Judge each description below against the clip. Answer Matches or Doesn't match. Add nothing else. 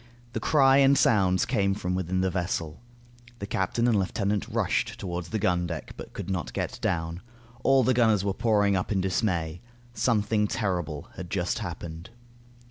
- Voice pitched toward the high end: Doesn't match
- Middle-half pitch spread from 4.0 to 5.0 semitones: Doesn't match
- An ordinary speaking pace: Matches